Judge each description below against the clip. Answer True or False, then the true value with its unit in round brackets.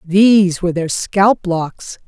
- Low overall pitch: False (185 Hz)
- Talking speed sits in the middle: True (145 wpm)